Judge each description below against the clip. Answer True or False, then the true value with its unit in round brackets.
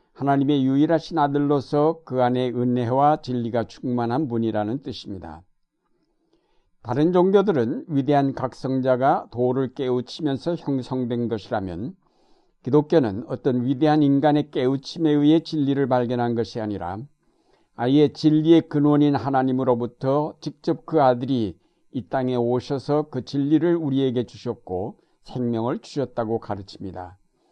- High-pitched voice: False (135 Hz)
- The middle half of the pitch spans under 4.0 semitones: True (3.4 semitones)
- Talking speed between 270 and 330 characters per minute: True (300 characters per minute)